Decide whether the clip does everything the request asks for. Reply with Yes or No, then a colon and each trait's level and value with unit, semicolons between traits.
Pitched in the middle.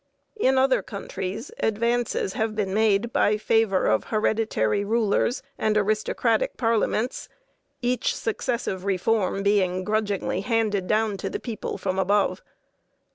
No: high, 215 Hz